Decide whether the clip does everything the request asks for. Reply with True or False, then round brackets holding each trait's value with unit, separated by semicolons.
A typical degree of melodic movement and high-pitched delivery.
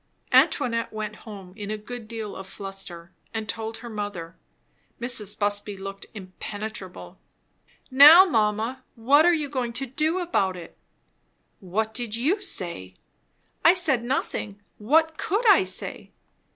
True (5.0 semitones; 220 Hz)